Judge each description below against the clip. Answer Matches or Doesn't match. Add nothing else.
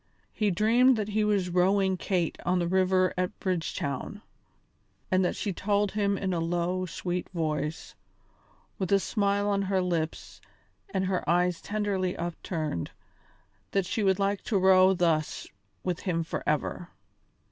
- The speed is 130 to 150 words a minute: Matches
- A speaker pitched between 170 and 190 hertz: Matches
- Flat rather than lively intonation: Matches